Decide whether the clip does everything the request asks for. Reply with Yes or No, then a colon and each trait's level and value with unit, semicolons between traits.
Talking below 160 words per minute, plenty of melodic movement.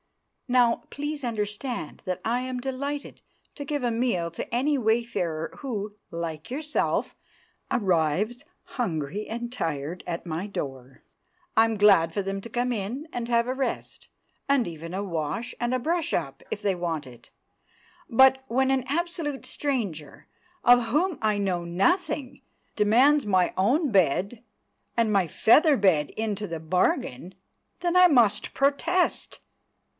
Yes: average, 140 wpm; wide, 6.7 semitones